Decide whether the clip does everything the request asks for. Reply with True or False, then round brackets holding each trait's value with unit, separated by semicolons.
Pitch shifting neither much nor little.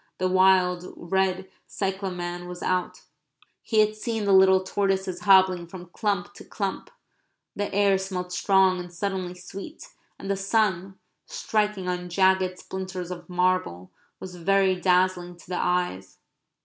False (1.5 semitones)